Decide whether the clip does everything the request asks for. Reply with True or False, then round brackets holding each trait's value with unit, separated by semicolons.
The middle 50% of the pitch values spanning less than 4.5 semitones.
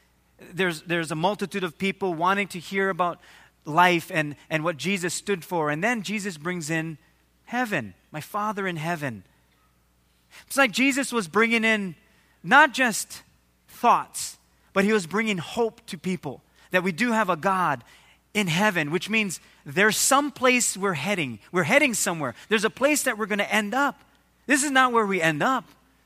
False (5.4 semitones)